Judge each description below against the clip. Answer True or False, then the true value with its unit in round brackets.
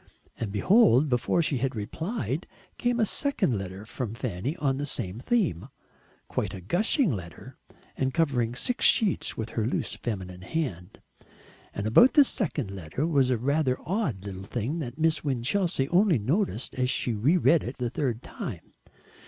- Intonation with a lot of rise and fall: True (7.2 semitones)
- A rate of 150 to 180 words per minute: True (165 wpm)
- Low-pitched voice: True (130 Hz)